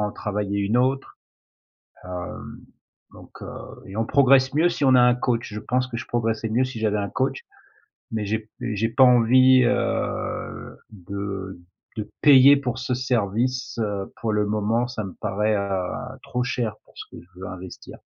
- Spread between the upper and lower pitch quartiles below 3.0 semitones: No, average, 3.8 semitones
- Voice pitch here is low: Yes, low, 115 Hz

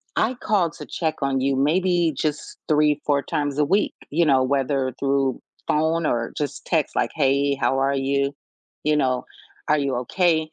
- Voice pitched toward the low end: No, medium, 145 Hz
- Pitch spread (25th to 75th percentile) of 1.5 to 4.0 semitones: Yes, narrow, 2.6 semitones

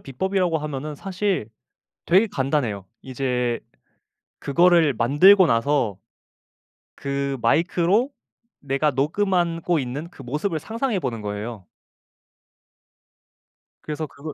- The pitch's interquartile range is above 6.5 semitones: No, average, 5.3 semitones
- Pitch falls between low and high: Yes, medium, 150 Hz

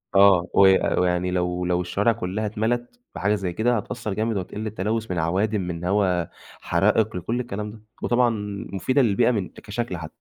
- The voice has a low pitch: Yes, low, 100 Hz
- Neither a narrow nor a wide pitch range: Yes, average, 3.5 semitones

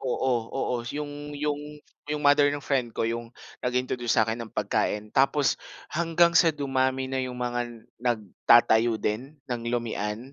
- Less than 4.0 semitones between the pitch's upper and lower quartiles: Yes, average, 3.5 semitones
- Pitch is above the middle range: No, low, 125 Hz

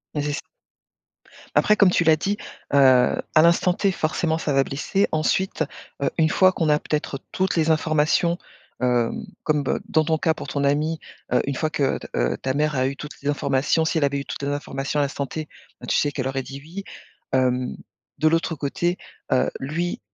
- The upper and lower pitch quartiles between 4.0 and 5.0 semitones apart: No, average, 2.8 semitones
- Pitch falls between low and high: Yes, medium, 150 Hz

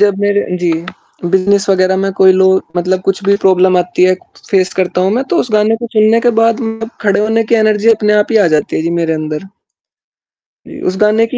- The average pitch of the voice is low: No, high, 200 Hz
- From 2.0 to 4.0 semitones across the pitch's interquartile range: Yes, average, 2.7 semitones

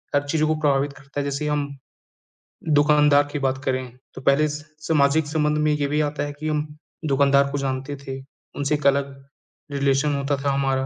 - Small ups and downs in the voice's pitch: Yes, narrow, 1.4 semitones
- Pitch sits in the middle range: Yes, medium, 145 Hz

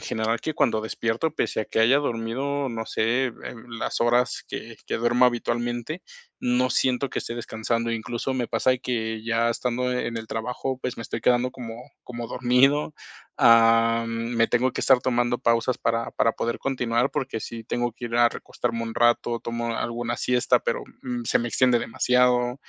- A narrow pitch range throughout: Yes, narrow, 1.5 semitones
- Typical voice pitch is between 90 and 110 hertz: No, low, 120 Hz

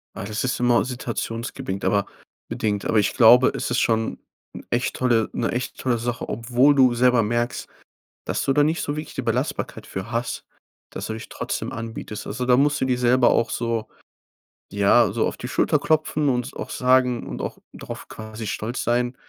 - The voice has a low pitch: Yes, low, 120 Hz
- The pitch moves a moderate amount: No, narrow, 2.1 semitones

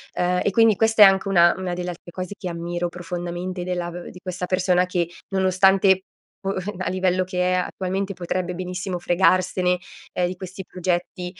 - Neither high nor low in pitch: Yes, medium, 180 Hz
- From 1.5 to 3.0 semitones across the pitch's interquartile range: No, narrow, 1.1 semitones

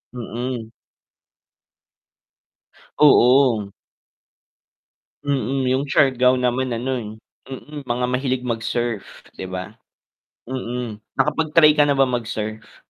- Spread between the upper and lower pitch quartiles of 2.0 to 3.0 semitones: Yes, average, 2.7 semitones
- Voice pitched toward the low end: Yes, low, 125 Hz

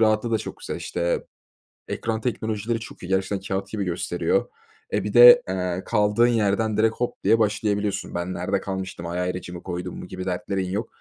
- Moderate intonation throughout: Yes, average, 3.3 semitones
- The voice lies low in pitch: Yes, low, 100 Hz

